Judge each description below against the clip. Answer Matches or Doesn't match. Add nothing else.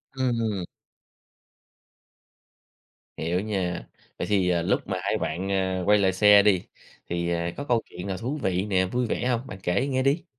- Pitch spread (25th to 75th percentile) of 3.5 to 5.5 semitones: Matches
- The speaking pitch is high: Doesn't match